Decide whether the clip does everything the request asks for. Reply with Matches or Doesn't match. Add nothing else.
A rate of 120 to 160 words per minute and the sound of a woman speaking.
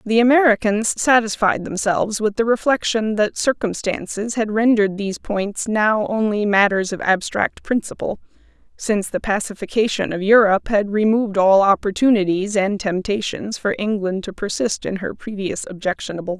Matches